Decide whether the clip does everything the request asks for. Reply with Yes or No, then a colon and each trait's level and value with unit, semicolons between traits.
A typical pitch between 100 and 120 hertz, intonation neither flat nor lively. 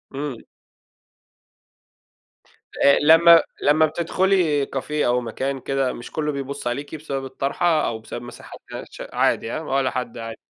No: medium, 140 Hz; average, 3.5 semitones